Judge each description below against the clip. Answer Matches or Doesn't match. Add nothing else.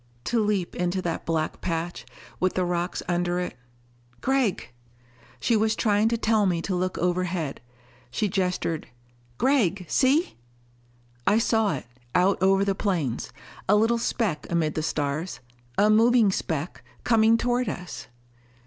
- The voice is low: Doesn't match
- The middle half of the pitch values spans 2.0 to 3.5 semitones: Doesn't match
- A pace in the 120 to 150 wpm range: Matches